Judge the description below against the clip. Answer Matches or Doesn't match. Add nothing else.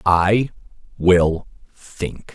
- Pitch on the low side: Matches